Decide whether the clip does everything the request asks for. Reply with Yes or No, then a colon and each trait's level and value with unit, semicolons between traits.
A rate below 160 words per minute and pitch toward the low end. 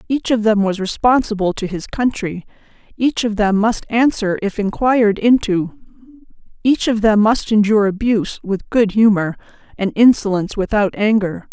No: average, 150 wpm; high, 215 Hz